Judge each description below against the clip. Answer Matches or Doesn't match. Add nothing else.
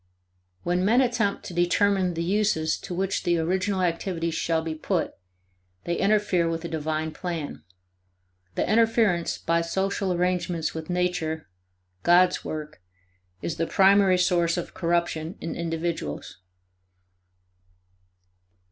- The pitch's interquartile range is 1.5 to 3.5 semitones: Matches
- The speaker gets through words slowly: Matches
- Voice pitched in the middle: Matches